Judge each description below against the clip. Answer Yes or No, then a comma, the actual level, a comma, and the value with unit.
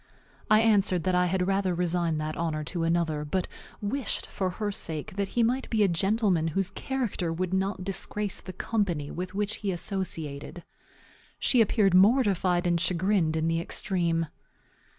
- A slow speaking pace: No, average, 165 wpm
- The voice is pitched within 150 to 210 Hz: Yes, medium, 185 Hz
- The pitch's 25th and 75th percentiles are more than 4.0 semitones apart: No, average, 3.3 semitones